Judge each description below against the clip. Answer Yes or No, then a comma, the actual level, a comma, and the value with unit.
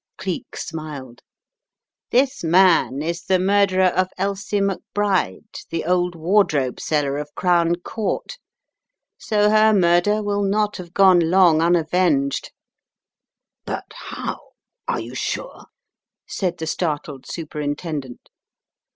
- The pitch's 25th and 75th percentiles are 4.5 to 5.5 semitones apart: No, average, 4.1 semitones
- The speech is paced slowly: Yes, slow, 115 wpm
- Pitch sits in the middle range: Yes, medium, 175 Hz